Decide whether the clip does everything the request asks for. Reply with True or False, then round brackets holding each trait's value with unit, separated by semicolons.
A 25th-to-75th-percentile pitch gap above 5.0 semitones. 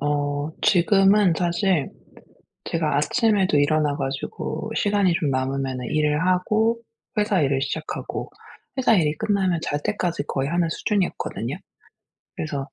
True (5.4 semitones)